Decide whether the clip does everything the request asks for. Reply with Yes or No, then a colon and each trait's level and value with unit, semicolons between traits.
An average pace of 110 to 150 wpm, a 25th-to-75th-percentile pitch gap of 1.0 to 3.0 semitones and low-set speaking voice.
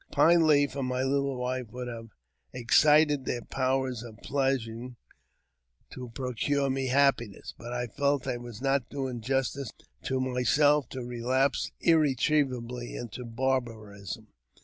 Yes: slow, 135 wpm; narrow, 2.5 semitones; low, 130 Hz